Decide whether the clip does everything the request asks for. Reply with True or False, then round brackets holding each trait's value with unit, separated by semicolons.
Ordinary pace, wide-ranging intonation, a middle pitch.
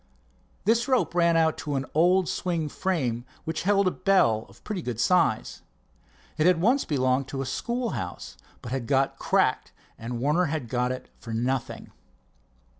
True (170 wpm; 6.3 semitones; 155 Hz)